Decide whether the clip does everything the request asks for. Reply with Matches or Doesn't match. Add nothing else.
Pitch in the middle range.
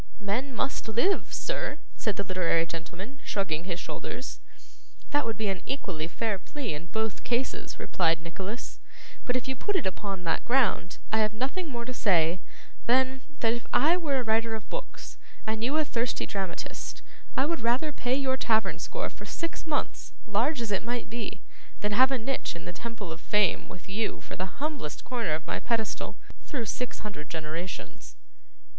Doesn't match